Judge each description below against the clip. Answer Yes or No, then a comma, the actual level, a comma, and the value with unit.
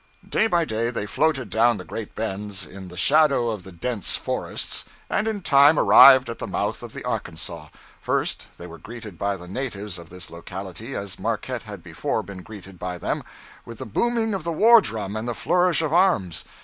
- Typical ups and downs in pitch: No, wide, 7.6 semitones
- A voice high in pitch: No, low, 110 Hz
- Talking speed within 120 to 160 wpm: No, average, 200 wpm